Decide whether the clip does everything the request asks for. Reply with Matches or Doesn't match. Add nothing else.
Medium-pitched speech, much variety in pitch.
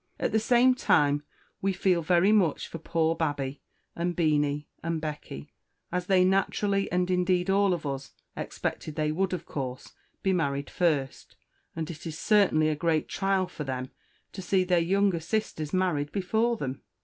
Doesn't match